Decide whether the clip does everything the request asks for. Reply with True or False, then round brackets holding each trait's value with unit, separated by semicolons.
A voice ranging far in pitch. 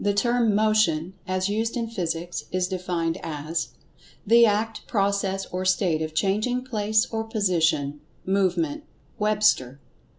False (4.2 semitones)